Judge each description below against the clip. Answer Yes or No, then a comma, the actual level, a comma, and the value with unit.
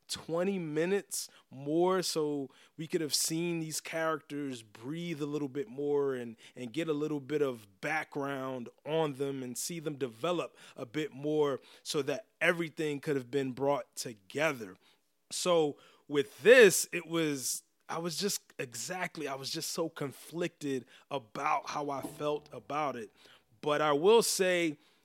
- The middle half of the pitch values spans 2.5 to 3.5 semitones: Yes, average, 3.0 semitones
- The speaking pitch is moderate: Yes, medium, 150 Hz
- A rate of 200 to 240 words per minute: No, average, 155 wpm